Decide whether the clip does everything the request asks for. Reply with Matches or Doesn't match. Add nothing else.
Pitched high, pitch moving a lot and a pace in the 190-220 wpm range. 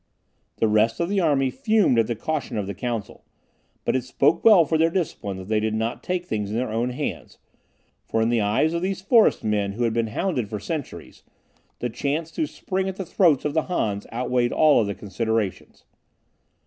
Doesn't match